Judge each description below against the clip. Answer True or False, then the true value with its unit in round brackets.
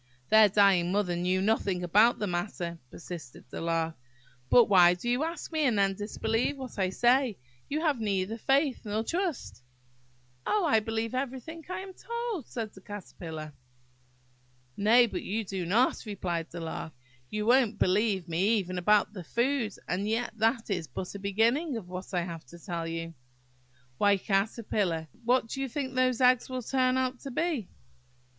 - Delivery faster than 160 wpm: True (175 wpm)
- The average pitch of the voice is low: False (215 Hz)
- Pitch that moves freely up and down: True (5.7 semitones)